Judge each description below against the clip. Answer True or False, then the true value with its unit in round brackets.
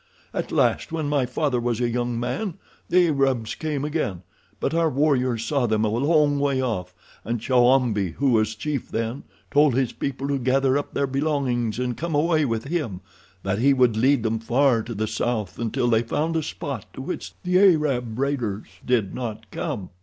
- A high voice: False (125 Hz)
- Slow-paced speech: False (185 wpm)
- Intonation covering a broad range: False (4.1 semitones)